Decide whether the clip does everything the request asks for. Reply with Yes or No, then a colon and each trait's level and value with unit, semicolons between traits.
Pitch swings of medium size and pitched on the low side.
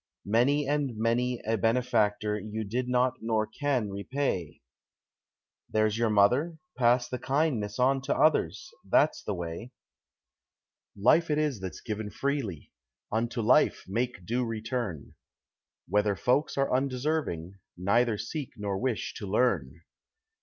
Yes: average, 3.9 semitones; low, 115 Hz